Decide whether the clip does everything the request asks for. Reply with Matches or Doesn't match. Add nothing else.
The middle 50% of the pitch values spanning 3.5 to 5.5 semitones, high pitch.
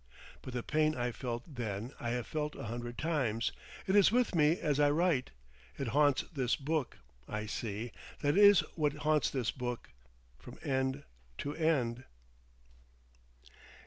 Doesn't match